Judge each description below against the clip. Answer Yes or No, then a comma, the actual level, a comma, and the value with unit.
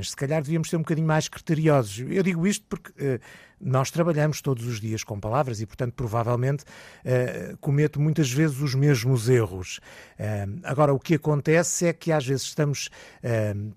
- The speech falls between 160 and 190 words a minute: Yes, average, 180 wpm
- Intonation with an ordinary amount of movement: Yes, average, 4.7 semitones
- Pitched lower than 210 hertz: Yes, medium, 140 Hz